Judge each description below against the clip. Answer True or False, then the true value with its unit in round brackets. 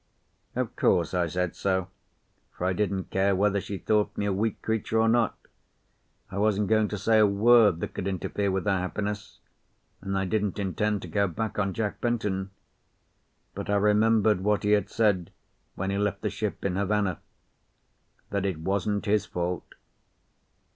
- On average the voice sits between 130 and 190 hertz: False (100 Hz)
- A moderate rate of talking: True (175 wpm)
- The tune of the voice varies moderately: False (1.8 semitones)